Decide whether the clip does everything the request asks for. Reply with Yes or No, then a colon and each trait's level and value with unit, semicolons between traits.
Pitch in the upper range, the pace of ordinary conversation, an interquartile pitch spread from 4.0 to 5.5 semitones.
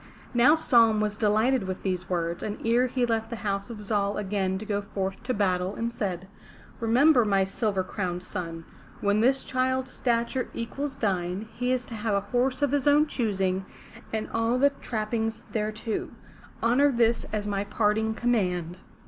No: high, 220 Hz; average, 175 wpm; average, 3.6 semitones